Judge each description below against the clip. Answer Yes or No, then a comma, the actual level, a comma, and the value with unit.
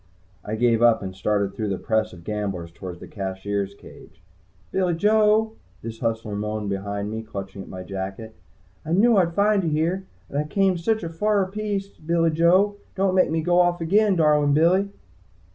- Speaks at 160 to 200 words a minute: Yes, average, 185 wpm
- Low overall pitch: No, medium, 150 Hz